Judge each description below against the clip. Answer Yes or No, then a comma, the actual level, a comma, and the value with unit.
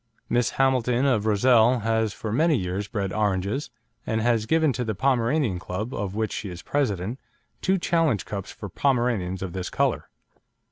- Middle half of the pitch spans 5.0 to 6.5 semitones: No, average, 4.4 semitones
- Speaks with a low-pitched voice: Yes, low, 110 Hz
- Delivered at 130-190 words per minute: Yes, average, 170 wpm